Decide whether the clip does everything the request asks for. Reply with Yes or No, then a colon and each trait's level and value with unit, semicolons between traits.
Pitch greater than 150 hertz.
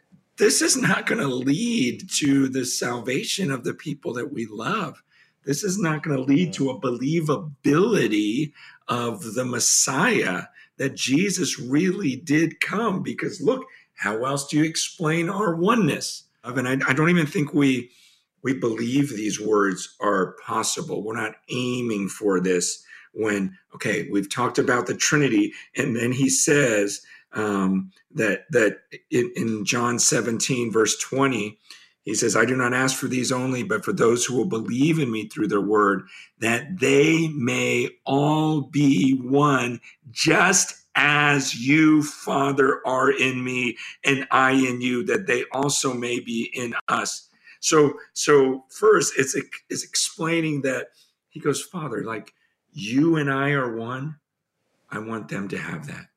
No: low, 135 Hz